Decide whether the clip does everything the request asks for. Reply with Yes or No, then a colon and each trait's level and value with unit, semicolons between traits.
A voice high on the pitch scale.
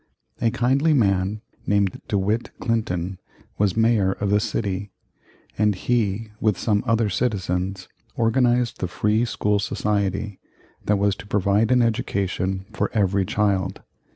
No: low, 105 Hz